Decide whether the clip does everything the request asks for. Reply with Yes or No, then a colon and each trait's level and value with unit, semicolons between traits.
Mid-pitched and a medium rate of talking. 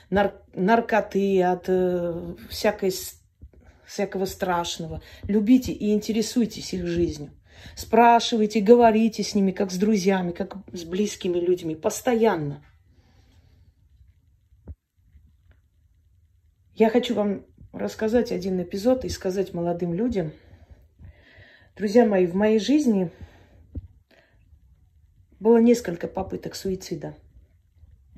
No: medium, 180 Hz; slow, 95 wpm